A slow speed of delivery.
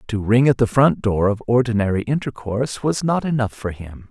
No: fast, 205 wpm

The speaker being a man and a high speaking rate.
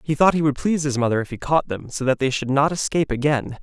Yes: male; fast, 300 wpm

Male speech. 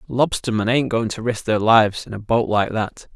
Yes: male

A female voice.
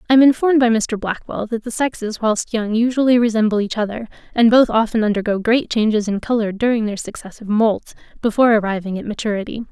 Yes: female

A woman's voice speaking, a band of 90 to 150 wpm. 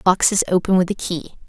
No: female; fast, 205 wpm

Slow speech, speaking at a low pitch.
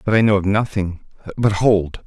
No: fast, 205 wpm; low, 100 Hz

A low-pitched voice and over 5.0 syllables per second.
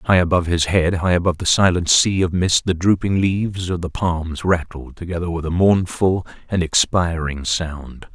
No: very low, 90 Hz; 4.9 syllables/s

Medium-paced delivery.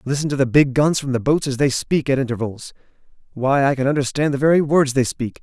No: fast, 245 wpm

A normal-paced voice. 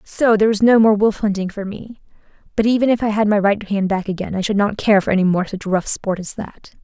No: fast, 270 wpm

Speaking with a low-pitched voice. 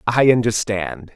Yes: low, 110 Hz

